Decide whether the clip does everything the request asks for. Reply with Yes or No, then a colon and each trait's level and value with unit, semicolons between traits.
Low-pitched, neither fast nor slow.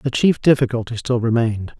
Yes: low, 120 Hz; average, 165 wpm